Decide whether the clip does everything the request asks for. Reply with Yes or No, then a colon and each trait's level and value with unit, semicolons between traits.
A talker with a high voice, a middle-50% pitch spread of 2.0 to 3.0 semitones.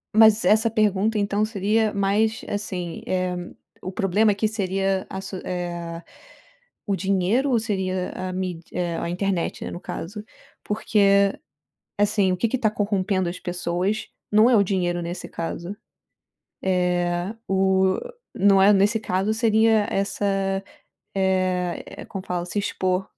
Yes: high, 195 Hz; narrow, 2.5 semitones